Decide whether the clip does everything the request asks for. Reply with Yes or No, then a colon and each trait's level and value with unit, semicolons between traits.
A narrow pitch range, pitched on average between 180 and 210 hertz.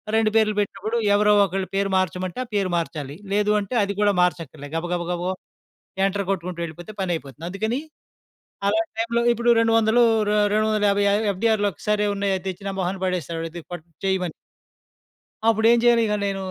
No: average, 3.3 semitones; high, 200 Hz